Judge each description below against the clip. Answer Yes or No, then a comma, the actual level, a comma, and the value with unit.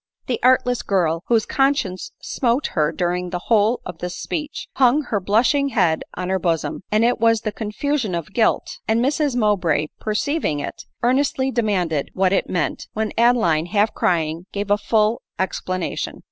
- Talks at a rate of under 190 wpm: Yes, average, 165 wpm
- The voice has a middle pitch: No, high, 210 Hz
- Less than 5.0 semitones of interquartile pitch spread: No, average, 5.3 semitones